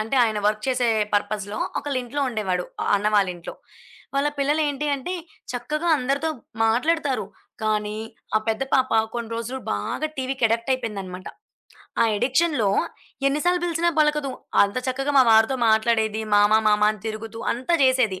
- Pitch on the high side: Yes, high, 240 Hz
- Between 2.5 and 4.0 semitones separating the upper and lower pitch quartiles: No, average, 4.4 semitones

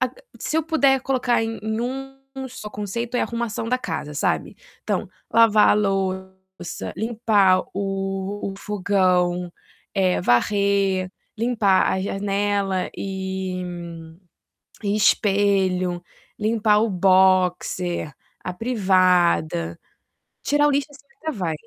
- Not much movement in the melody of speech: No, average, 3.5 semitones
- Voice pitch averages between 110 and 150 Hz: No, high, 200 Hz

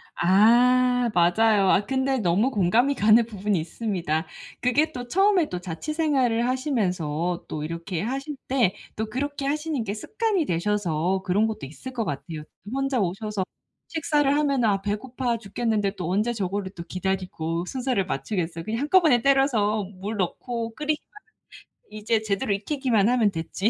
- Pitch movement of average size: No, wide, 5.7 semitones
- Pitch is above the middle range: Yes, high, 220 Hz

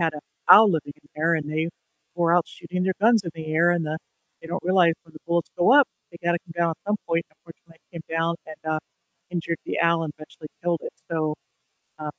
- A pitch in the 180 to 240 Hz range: No, medium, 165 Hz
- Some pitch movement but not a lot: No, narrow, 1.6 semitones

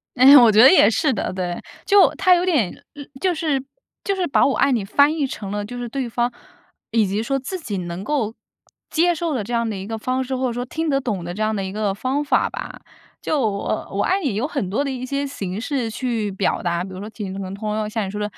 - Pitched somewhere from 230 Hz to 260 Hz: Yes, high, 235 Hz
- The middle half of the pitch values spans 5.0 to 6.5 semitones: Yes, average, 5.3 semitones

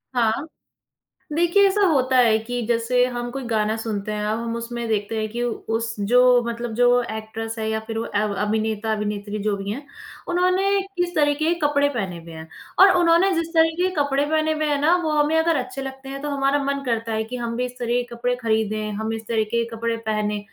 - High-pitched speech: Yes, high, 240 Hz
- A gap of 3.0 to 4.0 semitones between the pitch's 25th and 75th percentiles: No, average, 4.7 semitones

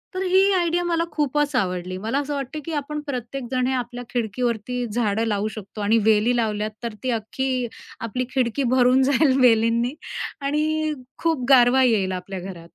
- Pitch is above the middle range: Yes, high, 245 Hz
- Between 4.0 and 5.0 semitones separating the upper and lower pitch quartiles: Yes, average, 4.3 semitones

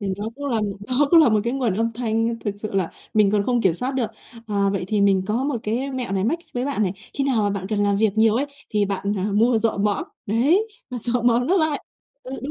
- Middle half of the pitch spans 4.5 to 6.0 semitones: No, average, 3.8 semitones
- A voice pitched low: No, high, 225 Hz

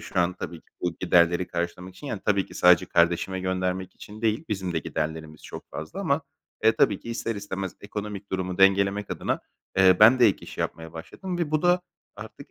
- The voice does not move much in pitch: No, average, 3.3 semitones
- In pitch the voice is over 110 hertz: No, very low, 95 Hz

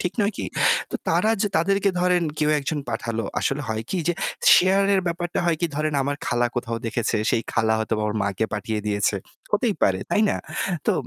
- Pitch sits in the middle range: Yes, medium, 145 Hz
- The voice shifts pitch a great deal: Yes, wide, 8.3 semitones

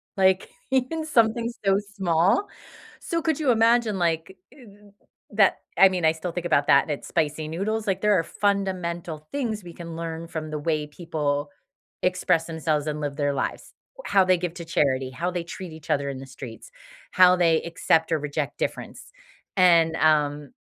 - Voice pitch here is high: No, medium, 170 Hz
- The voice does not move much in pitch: No, average, 4.2 semitones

